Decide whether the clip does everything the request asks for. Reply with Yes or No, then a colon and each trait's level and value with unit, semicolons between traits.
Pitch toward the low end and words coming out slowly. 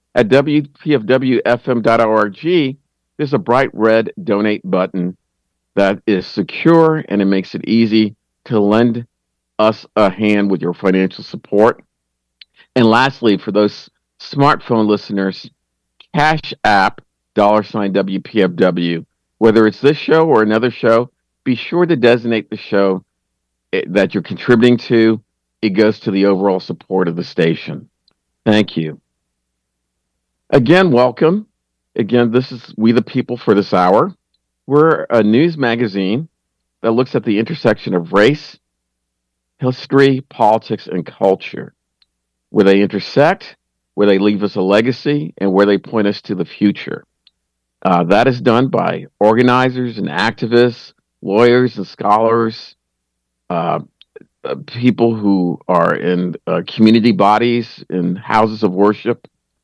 Yes: low, 105 Hz; slow, 130 wpm